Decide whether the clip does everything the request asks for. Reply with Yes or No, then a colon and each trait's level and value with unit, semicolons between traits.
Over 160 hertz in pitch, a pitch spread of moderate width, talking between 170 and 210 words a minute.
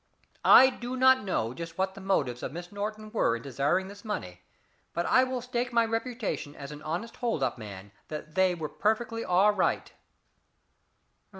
No: high, 190 Hz; wide, 7.5 semitones; average, 180 wpm